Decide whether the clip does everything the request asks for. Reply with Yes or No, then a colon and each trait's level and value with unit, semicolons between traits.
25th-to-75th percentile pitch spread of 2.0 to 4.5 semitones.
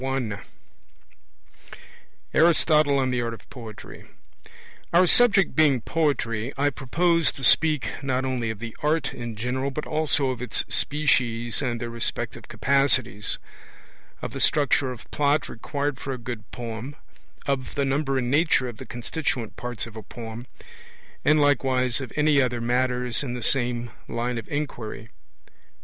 Yes: average, 3.4 semitones